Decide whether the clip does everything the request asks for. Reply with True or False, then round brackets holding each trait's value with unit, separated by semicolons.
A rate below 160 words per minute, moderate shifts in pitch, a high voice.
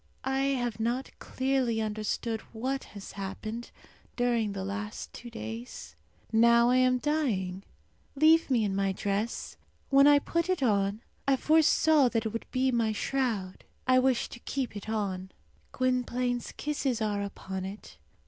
True (150 wpm; 4.3 semitones; 235 Hz)